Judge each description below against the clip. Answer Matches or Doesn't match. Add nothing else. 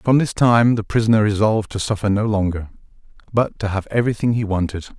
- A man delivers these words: Matches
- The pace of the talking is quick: Doesn't match